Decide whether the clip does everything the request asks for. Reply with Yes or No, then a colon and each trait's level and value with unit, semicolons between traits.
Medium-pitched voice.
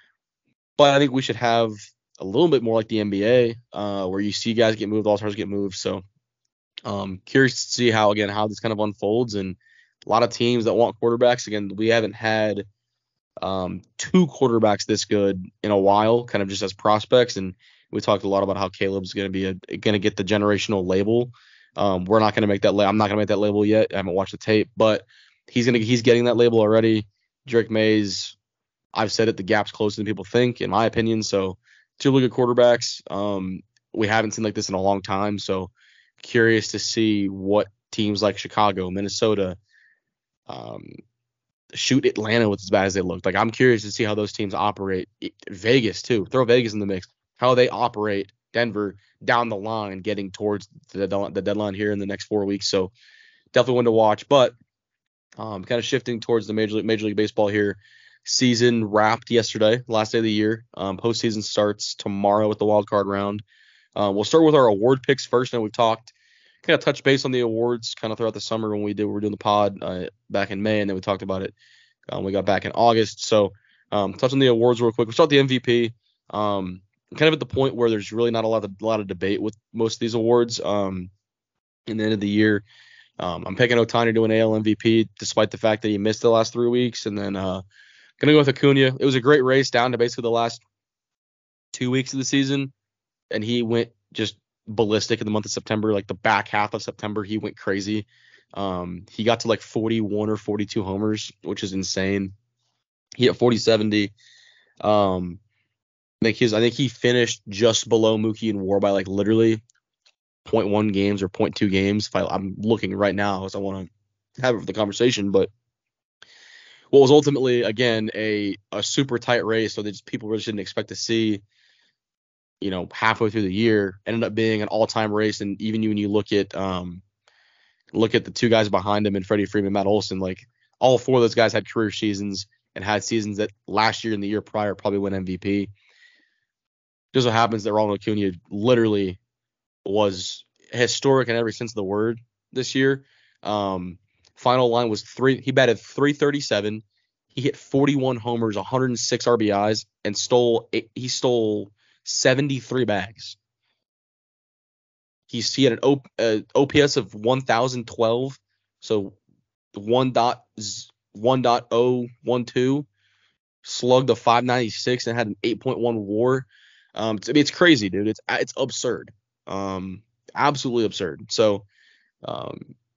No: low, 110 Hz